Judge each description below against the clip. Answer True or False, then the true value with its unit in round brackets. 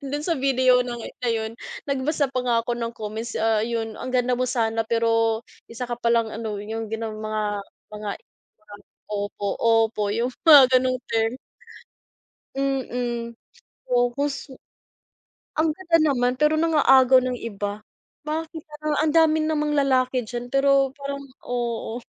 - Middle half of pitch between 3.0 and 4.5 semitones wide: True (3.3 semitones)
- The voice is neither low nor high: False (245 Hz)